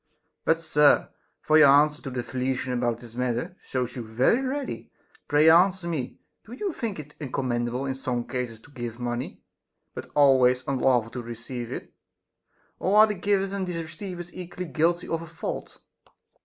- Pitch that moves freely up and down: Yes, wide, 5.8 semitones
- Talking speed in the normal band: Yes, average, 175 wpm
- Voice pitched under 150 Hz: Yes, medium, 140 Hz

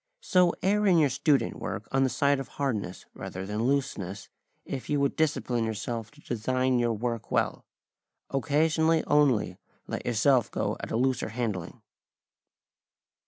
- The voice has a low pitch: Yes, low, 130 Hz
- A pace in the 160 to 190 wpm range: No, average, 150 wpm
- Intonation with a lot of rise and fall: No, average, 4.4 semitones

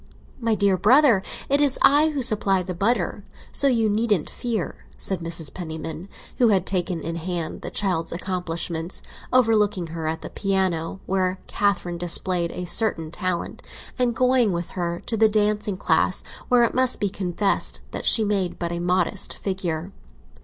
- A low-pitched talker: No, high, 190 Hz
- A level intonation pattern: No, average, 4.1 semitones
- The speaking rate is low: No, average, 165 wpm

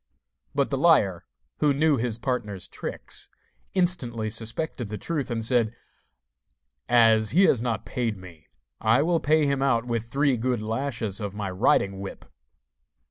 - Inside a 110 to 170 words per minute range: Yes, average, 150 wpm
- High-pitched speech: No, low, 120 Hz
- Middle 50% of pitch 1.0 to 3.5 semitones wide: No, average, 4.1 semitones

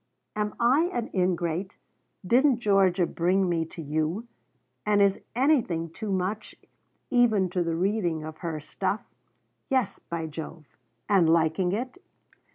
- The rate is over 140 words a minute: No, slow, 135 wpm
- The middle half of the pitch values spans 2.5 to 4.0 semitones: No, average, 4.5 semitones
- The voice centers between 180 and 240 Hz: Yes, medium, 185 Hz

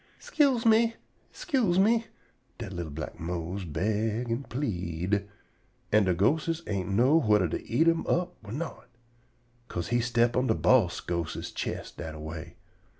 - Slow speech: No, average, 160 wpm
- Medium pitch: No, low, 110 Hz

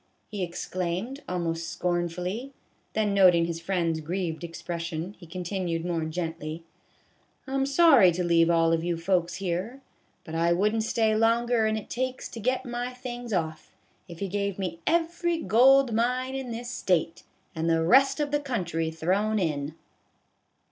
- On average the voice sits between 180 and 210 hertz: Yes, medium, 185 Hz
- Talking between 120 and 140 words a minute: No, average, 165 wpm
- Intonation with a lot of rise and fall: Yes, wide, 6.2 semitones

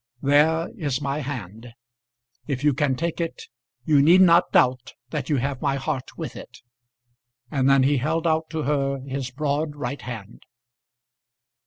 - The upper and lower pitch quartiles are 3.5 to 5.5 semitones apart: No, average, 2.8 semitones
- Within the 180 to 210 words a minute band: No, average, 160 wpm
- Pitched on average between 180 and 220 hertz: No, medium, 140 Hz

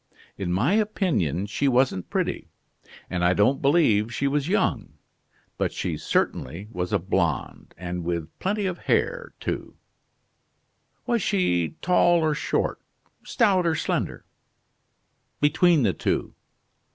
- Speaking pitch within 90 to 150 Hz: Yes, medium, 140 Hz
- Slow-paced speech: Yes, slow, 125 wpm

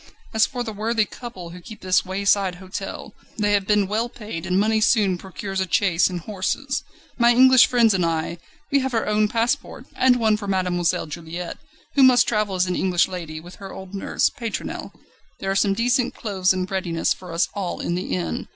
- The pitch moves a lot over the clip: No, average, 3.6 semitones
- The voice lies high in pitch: Yes, high, 195 Hz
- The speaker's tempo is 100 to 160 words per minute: No, fast, 205 wpm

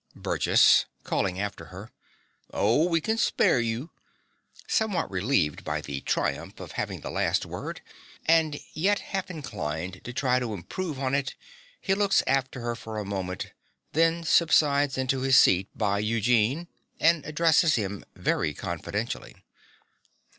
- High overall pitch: No, low, 130 Hz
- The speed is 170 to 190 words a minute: No, average, 140 wpm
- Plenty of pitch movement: Yes, wide, 7.9 semitones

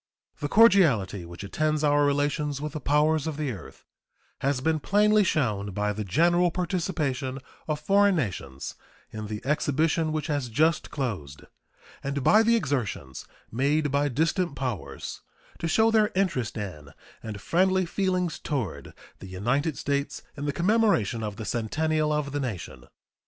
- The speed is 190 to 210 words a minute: No, average, 150 wpm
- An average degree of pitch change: No, wide, 6.4 semitones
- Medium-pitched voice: Yes, medium, 145 Hz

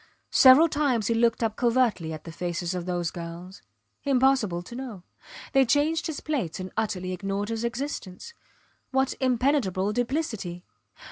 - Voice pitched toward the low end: No, high, 225 Hz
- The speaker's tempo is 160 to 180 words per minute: No, average, 145 wpm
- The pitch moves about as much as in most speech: No, wide, 6.5 semitones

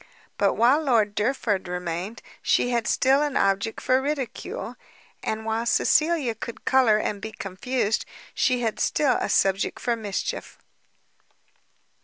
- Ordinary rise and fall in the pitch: Yes, average, 4.1 semitones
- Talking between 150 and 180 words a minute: No, slow, 135 wpm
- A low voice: No, high, 225 Hz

